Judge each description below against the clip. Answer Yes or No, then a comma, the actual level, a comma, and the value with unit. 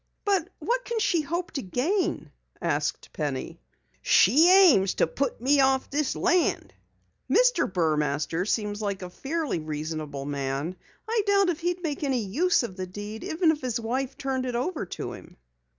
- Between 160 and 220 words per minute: Yes, average, 165 wpm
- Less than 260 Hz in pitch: No, very high, 265 Hz